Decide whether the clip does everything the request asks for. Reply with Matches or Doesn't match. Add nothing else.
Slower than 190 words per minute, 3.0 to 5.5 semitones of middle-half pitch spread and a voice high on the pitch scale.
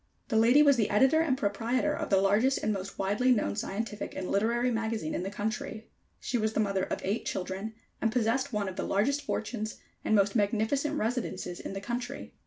Doesn't match